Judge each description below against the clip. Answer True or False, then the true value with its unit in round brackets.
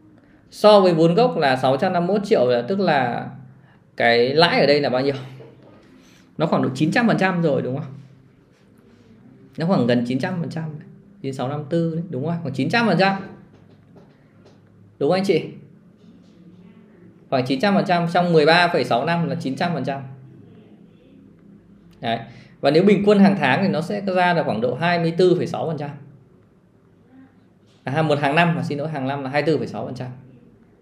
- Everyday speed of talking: False (155 wpm)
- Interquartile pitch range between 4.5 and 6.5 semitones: True (5.4 semitones)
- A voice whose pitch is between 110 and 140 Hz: False (165 Hz)